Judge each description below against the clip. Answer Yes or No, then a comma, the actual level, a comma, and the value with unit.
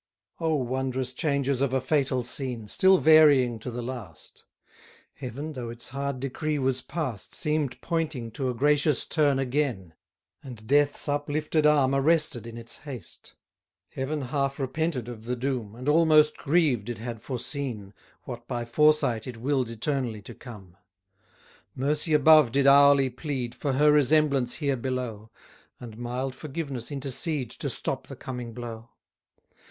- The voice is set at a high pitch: No, low, 135 Hz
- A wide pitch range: No, average, 3.5 semitones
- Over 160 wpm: No, average, 145 wpm